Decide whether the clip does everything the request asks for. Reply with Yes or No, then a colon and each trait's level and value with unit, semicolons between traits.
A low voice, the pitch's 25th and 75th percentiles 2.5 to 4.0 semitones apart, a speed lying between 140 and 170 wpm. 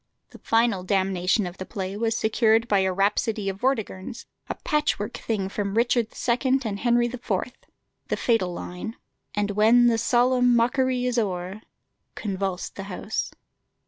No: high, 220 Hz; average, 3.6 semitones; average, 155 wpm